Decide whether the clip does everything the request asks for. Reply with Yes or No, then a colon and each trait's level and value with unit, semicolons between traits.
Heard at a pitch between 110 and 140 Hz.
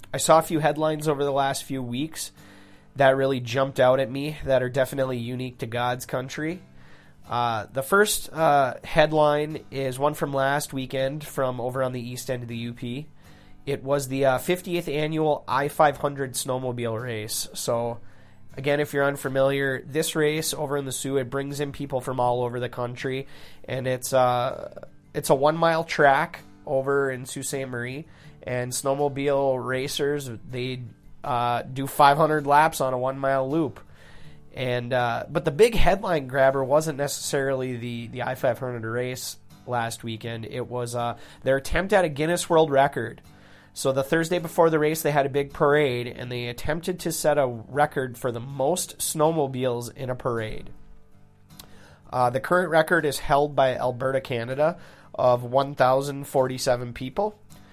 Yes: low, 135 Hz